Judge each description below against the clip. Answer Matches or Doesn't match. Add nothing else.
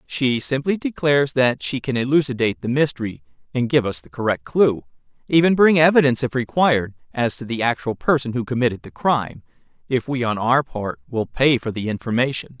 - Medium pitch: Doesn't match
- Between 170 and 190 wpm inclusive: Matches